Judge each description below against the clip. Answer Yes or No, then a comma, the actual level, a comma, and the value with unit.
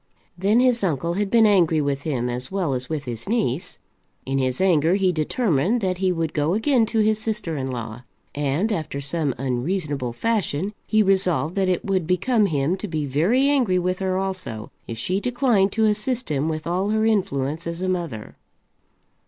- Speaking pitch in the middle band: Yes, medium, 180 Hz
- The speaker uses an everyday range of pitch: No, wide, 6.3 semitones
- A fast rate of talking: No, average, 190 wpm